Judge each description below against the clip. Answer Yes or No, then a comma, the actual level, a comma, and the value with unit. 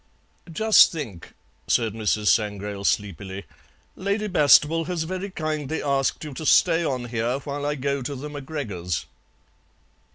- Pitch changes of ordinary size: No, wide, 6.6 semitones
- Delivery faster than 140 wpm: No, slow, 135 wpm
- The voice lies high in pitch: No, medium, 140 Hz